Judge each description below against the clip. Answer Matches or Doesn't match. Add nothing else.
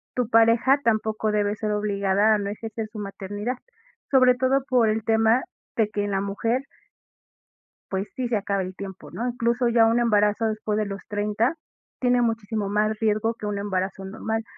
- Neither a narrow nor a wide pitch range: Doesn't match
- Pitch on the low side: Doesn't match